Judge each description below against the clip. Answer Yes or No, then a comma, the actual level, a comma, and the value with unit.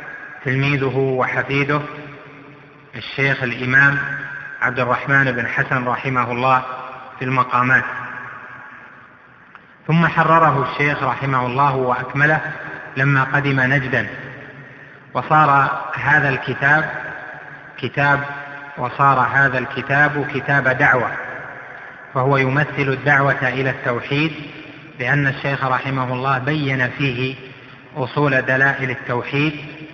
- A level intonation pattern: Yes, narrow, 2.3 semitones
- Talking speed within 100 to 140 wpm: No, average, 90 wpm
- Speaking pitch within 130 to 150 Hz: Yes, low, 135 Hz